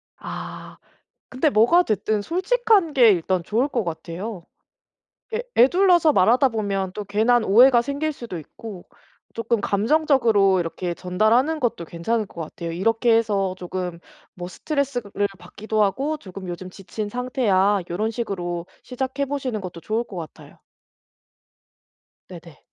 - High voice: Yes, high, 215 Hz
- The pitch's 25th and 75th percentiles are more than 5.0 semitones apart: Yes, wide, 5.6 semitones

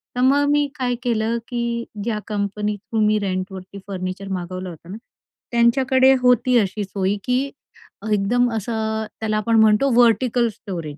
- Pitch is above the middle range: Yes, high, 220 Hz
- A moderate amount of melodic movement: Yes, average, 3.7 semitones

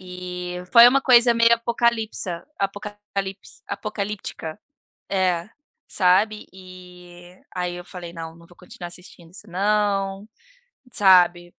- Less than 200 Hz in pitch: Yes, high, 190 Hz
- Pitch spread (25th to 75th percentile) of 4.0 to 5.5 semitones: No, average, 2.8 semitones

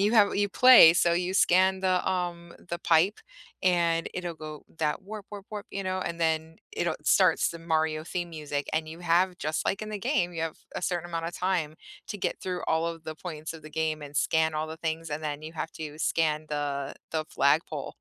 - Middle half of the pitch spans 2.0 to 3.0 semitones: Yes, narrow, 2.5 semitones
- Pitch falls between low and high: Yes, medium, 165 Hz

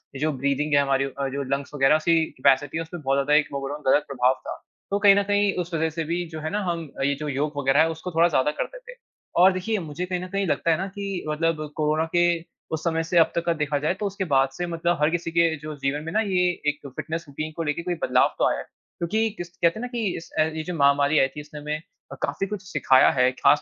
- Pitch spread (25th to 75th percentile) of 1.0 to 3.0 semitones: No, average, 3.6 semitones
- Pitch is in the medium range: Yes, medium, 160 Hz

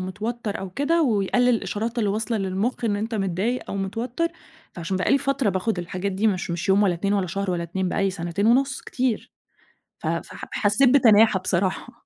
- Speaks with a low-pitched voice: No, high, 205 Hz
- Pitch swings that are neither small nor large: Yes, average, 4.0 semitones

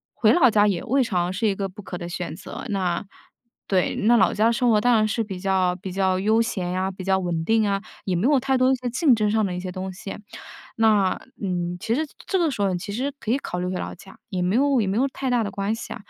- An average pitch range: Yes, average, 3.9 semitones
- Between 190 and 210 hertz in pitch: Yes, high, 205 Hz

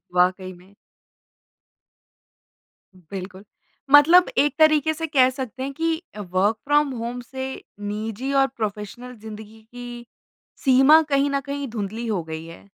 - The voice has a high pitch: Yes, high, 245 Hz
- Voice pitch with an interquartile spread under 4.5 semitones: No, average, 5.2 semitones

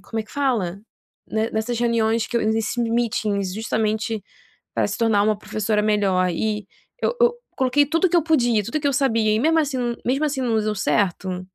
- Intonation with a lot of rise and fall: No, average, 3.4 semitones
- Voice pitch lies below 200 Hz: No, high, 225 Hz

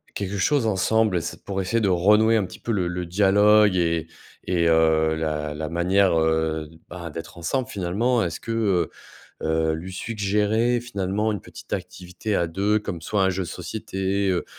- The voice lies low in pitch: Yes, very low, 95 Hz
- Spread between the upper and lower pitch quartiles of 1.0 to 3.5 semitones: No, average, 4.0 semitones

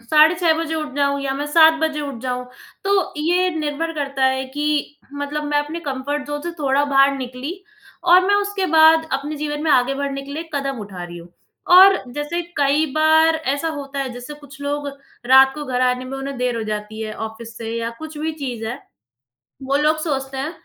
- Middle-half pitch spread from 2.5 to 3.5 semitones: Yes, average, 2.8 semitones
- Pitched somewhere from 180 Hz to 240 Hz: No, very high, 285 Hz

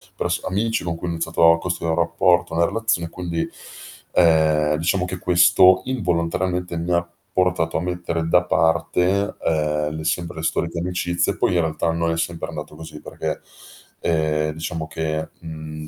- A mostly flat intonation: Yes, narrow, 1.7 semitones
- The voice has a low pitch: Yes, very low, 85 Hz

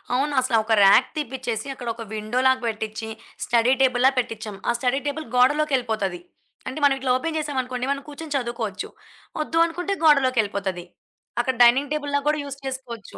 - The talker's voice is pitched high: Yes, very high, 255 Hz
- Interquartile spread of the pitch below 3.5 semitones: No, average, 3.8 semitones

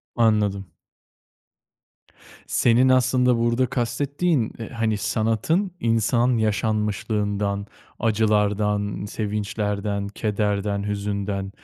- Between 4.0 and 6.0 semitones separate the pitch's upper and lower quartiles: No, narrow, 2.4 semitones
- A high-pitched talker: No, low, 105 Hz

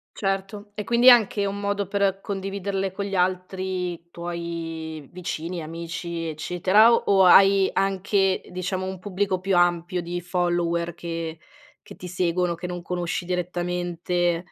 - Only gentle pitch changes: Yes, narrow, 2.2 semitones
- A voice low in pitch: No, medium, 180 Hz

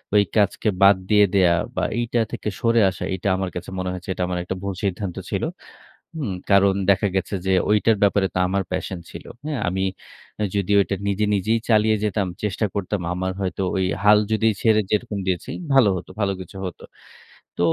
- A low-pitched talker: Yes, low, 100 Hz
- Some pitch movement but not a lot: No, narrow, 2.3 semitones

